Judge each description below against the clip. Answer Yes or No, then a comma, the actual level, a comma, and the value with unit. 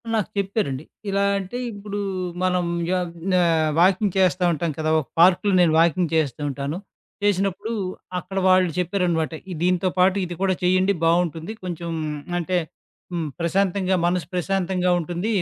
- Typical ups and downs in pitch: No, narrow, 2.3 semitones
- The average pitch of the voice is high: No, medium, 180 Hz